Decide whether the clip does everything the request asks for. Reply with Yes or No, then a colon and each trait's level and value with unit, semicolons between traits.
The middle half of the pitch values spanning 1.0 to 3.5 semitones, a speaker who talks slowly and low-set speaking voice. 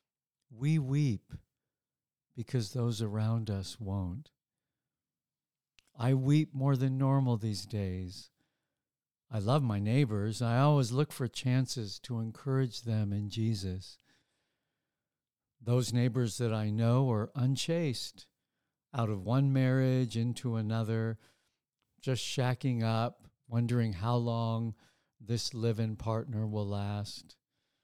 Yes: average, 3.1 semitones; slow, 115 wpm; low, 120 Hz